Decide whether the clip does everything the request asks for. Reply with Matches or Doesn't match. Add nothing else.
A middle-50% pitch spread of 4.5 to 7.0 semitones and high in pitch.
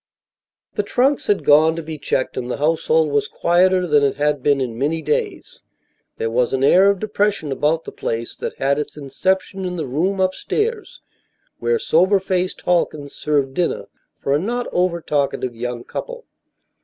Doesn't match